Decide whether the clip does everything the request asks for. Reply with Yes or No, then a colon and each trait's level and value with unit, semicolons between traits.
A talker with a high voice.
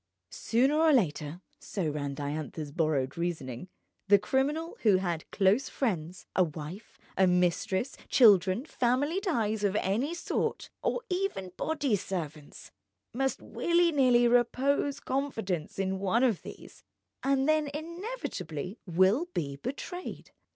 Yes: high, 210 Hz